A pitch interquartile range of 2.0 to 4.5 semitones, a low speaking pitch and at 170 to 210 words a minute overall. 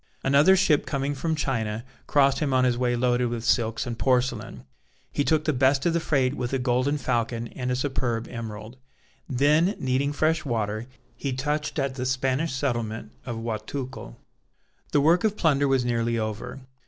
Yes: average, 3.3 semitones; low, 130 Hz; average, 175 wpm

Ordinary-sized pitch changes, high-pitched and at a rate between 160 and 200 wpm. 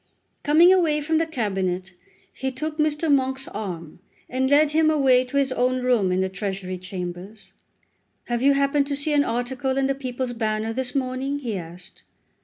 No: wide, 5.7 semitones; very high, 255 Hz; average, 180 wpm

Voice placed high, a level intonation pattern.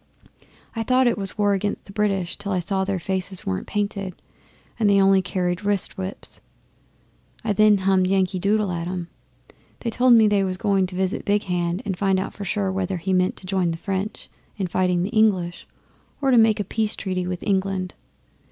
Yes: high, 195 Hz; narrow, 2.1 semitones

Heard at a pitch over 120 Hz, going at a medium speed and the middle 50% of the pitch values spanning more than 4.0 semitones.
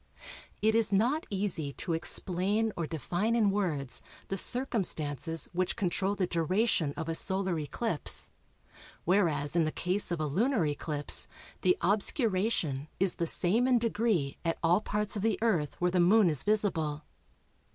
Yes: medium, 185 Hz; average, 155 wpm; average, 4.6 semitones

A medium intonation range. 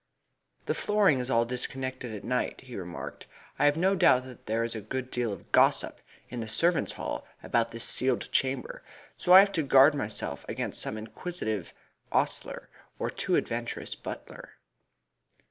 Yes: average, 4.1 semitones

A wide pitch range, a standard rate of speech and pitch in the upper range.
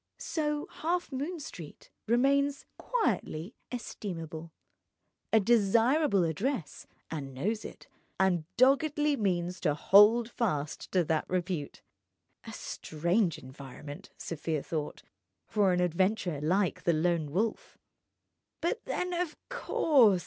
No: wide, 8.4 semitones; slow, 105 wpm; high, 195 Hz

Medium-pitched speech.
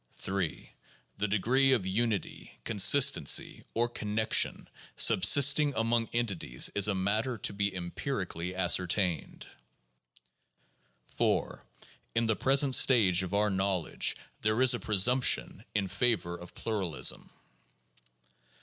No: low, 105 Hz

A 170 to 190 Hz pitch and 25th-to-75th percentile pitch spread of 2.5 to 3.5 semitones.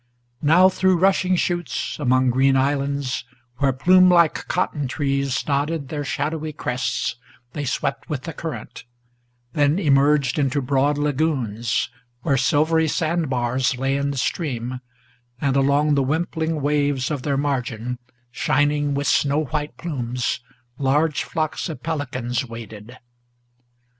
No: medium, 140 Hz; average, 2.9 semitones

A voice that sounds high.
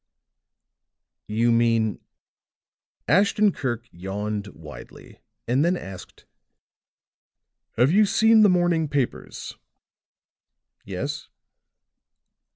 No: low, 120 Hz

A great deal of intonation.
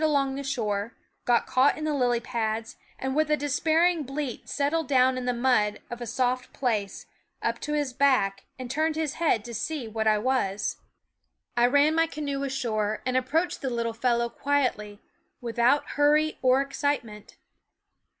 No: average, 3.7 semitones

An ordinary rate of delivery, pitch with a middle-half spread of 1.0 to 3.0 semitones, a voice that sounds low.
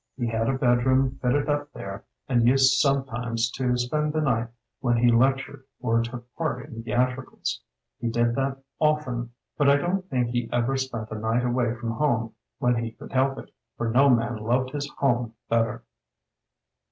Yes: average, 175 wpm; narrow, 2.5 semitones; low, 125 Hz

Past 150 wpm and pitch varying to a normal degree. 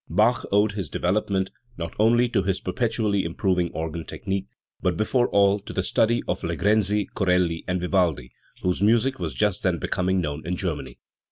Yes: average, 170 wpm; average, 3.3 semitones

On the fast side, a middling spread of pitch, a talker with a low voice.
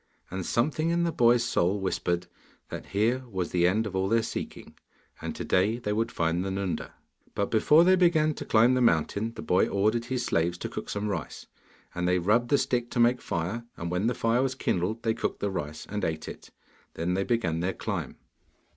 Yes: fast, 215 wpm; average, 5.0 semitones; low, 105 Hz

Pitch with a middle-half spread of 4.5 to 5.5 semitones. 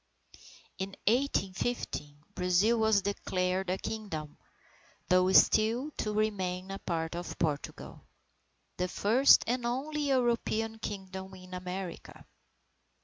No: average, 3.6 semitones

